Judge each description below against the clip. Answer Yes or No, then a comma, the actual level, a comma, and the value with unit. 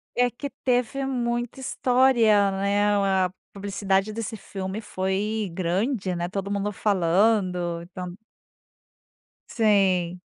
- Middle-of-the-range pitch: No, high, 200 Hz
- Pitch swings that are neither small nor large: Yes, average, 3.3 semitones